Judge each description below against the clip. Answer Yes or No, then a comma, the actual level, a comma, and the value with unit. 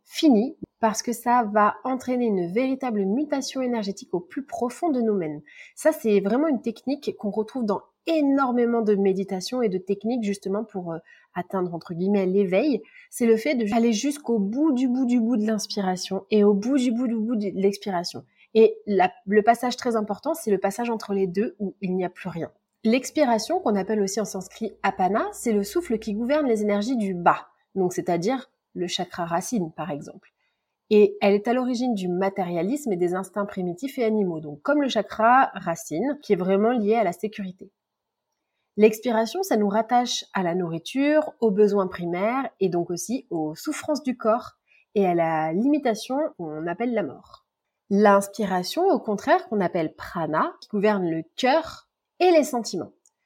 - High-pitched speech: Yes, high, 215 Hz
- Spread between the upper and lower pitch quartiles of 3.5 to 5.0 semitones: Yes, average, 4.5 semitones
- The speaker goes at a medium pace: Yes, average, 180 wpm